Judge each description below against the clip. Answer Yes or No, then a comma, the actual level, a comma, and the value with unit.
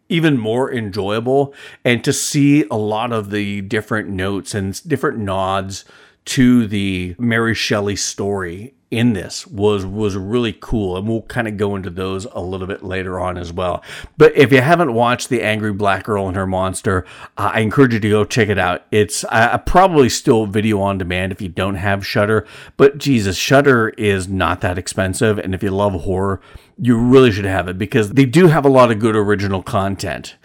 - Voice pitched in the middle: No, low, 105 Hz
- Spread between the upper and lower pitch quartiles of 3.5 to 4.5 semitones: Yes, average, 3.9 semitones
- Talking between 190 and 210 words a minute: Yes, average, 195 wpm